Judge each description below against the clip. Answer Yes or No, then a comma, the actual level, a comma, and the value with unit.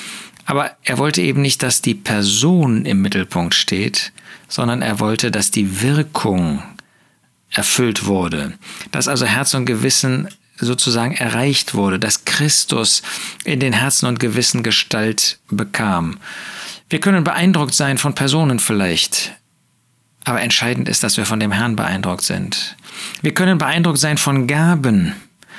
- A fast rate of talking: No, average, 140 wpm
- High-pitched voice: No, low, 125 Hz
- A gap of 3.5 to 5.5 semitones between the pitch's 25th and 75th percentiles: Yes, average, 4.7 semitones